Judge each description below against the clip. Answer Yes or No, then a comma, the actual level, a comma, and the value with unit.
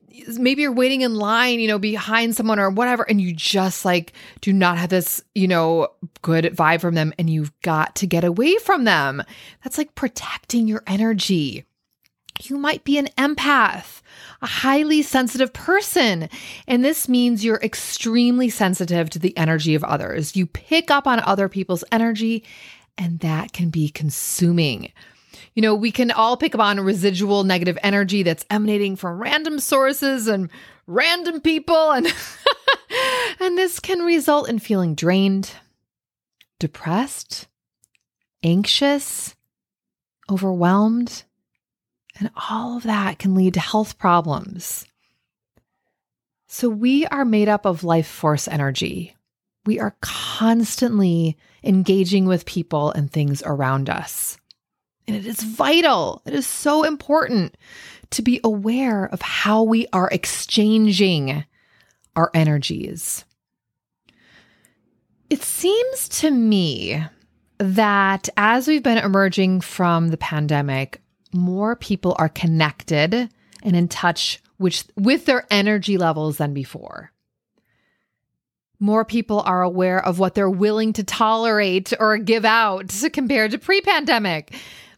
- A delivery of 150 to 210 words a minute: No, slow, 135 wpm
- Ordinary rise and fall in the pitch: No, wide, 5.7 semitones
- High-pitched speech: Yes, high, 205 Hz